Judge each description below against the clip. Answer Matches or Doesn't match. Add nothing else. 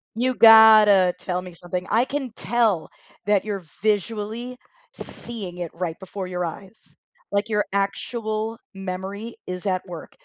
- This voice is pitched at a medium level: Doesn't match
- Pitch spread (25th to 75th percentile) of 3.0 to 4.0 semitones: Matches